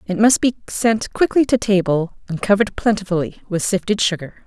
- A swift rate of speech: No, average, 175 wpm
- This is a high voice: Yes, high, 205 Hz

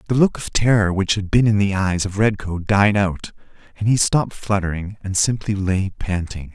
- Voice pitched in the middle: No, low, 100 Hz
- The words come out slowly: No, average, 200 wpm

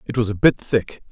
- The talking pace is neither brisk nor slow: No, fast, 270 wpm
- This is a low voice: Yes, low, 115 Hz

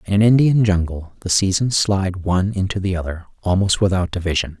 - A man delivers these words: Yes, male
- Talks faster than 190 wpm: No, average, 185 wpm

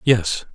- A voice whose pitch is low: Yes, low, 100 Hz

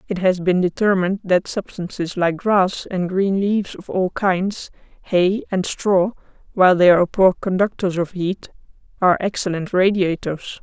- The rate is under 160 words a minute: Yes, average, 150 wpm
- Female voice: Yes, female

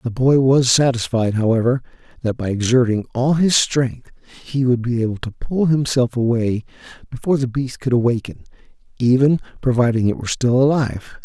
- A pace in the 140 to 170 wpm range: Yes, average, 160 wpm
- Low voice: Yes, low, 125 Hz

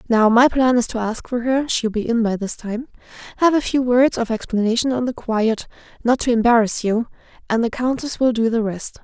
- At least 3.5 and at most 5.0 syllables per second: Yes, 4.9 syllables/s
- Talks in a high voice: Yes, high, 235 Hz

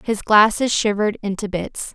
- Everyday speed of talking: Yes, average, 155 wpm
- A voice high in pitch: Yes, high, 210 Hz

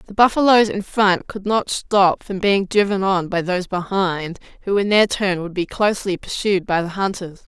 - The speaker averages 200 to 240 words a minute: No, average, 190 wpm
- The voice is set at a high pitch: Yes, high, 195 Hz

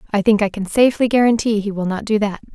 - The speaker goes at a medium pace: No, fast, 260 wpm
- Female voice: Yes, female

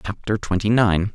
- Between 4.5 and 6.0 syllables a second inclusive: Yes, 5.0 syllables/s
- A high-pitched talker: No, low, 105 Hz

